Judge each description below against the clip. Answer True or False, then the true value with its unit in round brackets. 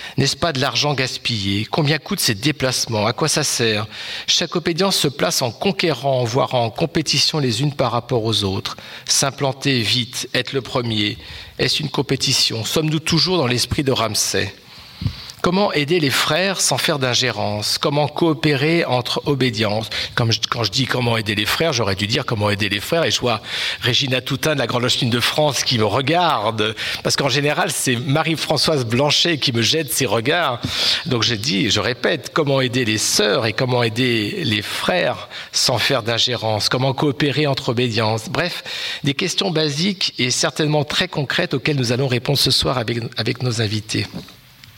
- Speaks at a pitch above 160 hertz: False (130 Hz)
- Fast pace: False (175 wpm)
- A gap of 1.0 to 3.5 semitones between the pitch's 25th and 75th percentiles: False (4.7 semitones)